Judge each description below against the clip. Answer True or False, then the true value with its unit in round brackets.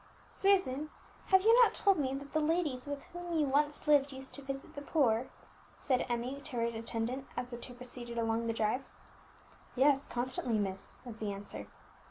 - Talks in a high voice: True (265 Hz)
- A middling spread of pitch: True (3.8 semitones)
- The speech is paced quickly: False (185 wpm)